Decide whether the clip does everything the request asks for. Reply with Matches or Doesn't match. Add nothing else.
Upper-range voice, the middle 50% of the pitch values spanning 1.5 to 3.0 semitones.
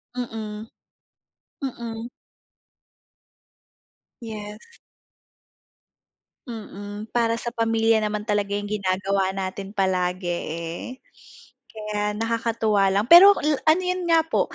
Matches